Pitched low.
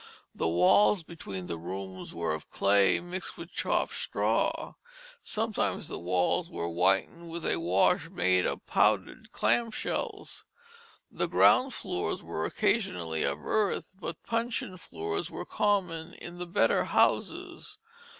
Yes: low, 100 Hz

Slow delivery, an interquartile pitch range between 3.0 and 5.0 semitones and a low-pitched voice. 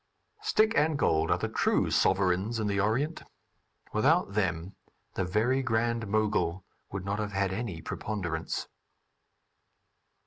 Yes: slow, 130 wpm; average, 3.9 semitones; low, 105 Hz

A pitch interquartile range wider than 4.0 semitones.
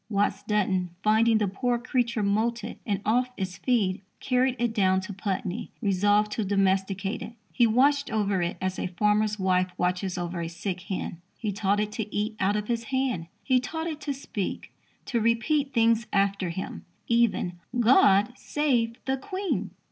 No: average, 3.7 semitones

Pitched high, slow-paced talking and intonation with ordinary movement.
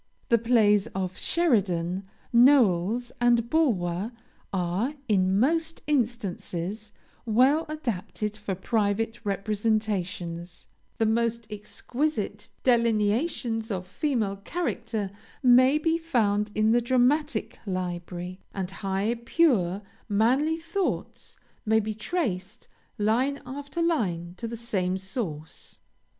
Yes: high, 220 Hz; slow, 105 wpm; average, 4.6 semitones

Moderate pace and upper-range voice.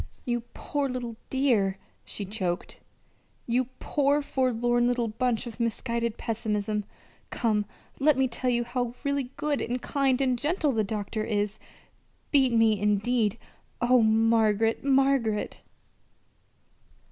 No: slow, 125 wpm; high, 235 Hz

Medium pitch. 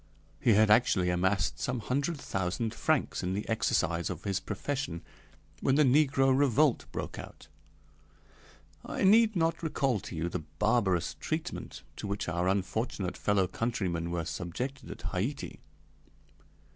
No: low, 105 Hz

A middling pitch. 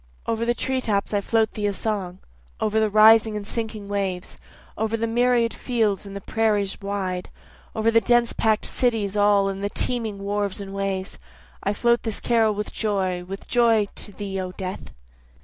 No: high, 210 Hz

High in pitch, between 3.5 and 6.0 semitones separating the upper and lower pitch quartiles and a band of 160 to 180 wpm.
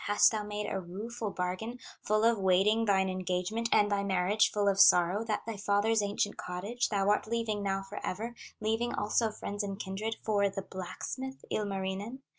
No: high, 205 Hz; narrow, 2.4 semitones; average, 175 wpm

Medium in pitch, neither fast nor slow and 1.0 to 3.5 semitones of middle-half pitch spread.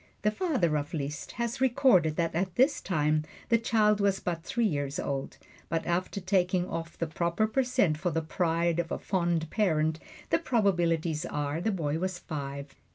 No: medium, 170 Hz; average, 180 wpm; average, 4.4 semitones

